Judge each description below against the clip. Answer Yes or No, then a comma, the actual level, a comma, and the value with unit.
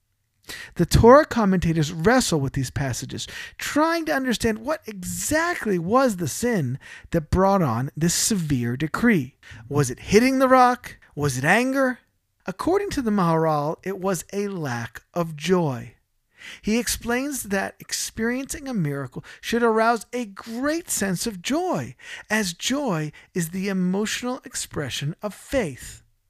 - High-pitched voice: Yes, high, 195 Hz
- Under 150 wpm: Yes, slow, 135 wpm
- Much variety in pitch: Yes, wide, 8.2 semitones